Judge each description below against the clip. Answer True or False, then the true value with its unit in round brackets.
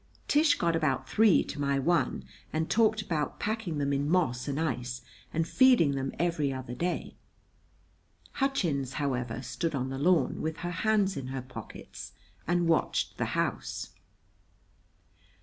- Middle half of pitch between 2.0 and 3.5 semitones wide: False (5.0 semitones)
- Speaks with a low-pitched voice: False (155 Hz)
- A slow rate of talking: False (150 wpm)